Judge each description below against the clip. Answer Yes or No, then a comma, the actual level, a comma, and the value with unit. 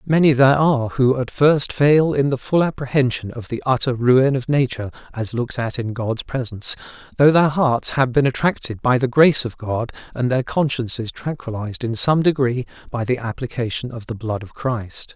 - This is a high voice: No, low, 125 Hz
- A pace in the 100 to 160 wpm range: No, average, 195 wpm